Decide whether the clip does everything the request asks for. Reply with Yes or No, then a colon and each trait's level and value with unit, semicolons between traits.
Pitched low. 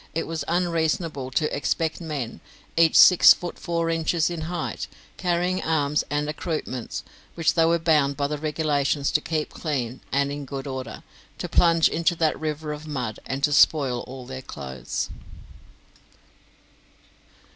No: medium, 155 Hz